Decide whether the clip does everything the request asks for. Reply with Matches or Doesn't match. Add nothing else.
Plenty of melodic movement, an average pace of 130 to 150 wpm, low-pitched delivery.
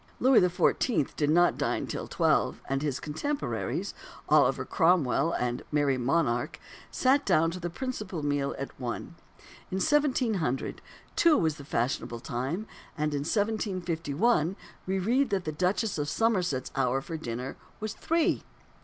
Doesn't match